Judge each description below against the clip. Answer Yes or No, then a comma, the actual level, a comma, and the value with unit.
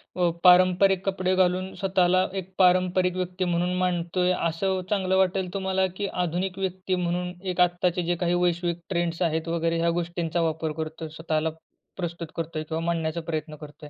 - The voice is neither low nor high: Yes, medium, 175 Hz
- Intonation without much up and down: Yes, narrow, 1.7 semitones